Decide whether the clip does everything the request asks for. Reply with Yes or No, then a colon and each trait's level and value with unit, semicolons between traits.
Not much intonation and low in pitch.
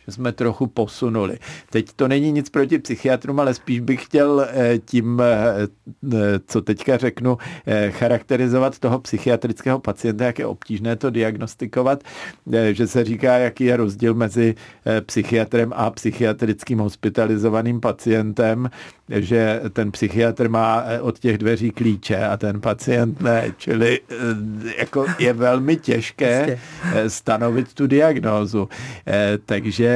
Yes: narrow, 2.3 semitones; low, 115 Hz